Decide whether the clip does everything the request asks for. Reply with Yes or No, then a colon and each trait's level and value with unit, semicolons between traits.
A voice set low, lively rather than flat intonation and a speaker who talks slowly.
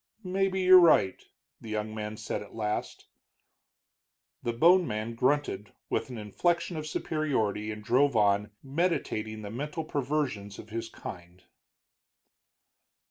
Yes: low, 115 Hz; wide, 6.5 semitones; slow, 130 wpm